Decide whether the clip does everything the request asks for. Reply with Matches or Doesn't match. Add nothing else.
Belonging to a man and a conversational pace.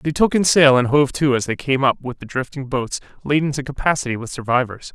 Doesn't match